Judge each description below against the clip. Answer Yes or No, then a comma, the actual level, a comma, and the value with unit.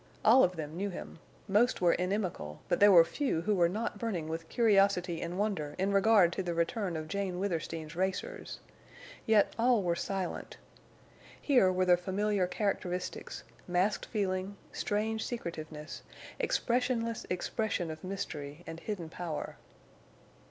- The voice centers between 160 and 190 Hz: Yes, medium, 185 Hz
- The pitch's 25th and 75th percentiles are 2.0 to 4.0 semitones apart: Yes, average, 3.6 semitones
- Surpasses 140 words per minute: No, slow, 135 wpm